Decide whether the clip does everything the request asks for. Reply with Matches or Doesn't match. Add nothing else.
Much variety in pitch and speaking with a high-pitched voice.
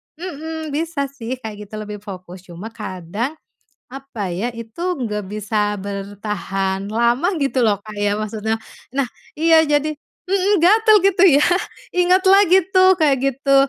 Matches